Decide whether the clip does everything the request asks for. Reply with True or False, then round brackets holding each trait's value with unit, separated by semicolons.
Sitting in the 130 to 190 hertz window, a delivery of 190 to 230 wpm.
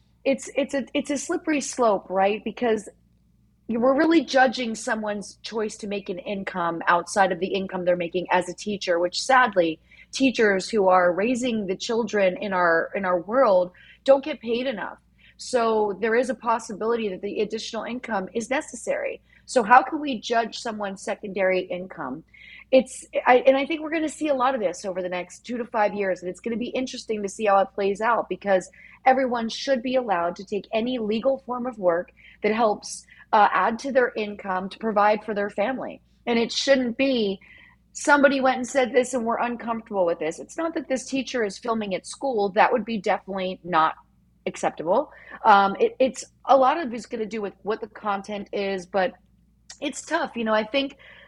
False (225 Hz; 200 wpm)